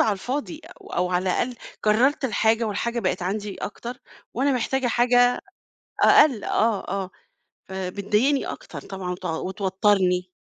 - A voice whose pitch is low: No, high, 210 Hz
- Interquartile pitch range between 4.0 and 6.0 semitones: Yes, average, 4.5 semitones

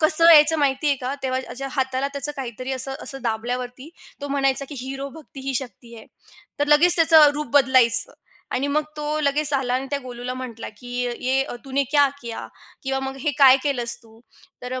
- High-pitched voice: Yes, very high, 270 Hz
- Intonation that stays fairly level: Yes, narrow, 2.3 semitones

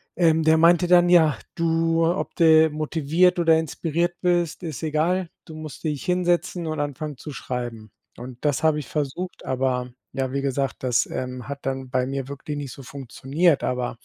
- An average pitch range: Yes, average, 3.8 semitones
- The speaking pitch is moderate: Yes, medium, 155 Hz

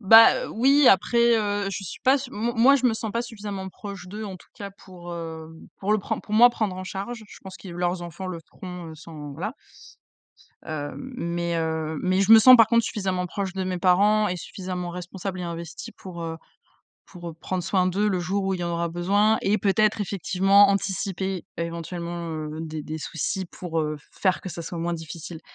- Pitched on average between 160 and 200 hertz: Yes, medium, 185 Hz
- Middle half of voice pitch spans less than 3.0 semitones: No, average, 3.3 semitones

